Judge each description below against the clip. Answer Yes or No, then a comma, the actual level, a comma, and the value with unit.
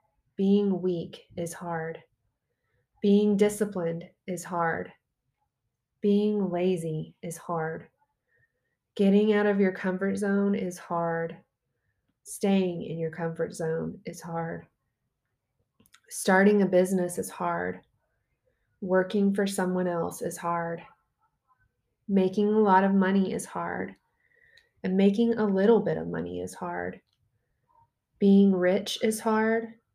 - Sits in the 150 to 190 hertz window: Yes, medium, 185 Hz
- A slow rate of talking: Yes, slow, 115 wpm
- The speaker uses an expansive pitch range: No, average, 3.7 semitones